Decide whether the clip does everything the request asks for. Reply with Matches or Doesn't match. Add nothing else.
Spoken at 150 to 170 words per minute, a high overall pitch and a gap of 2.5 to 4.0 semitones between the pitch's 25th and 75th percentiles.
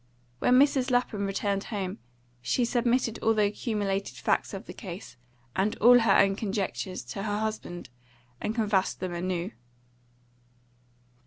Doesn't match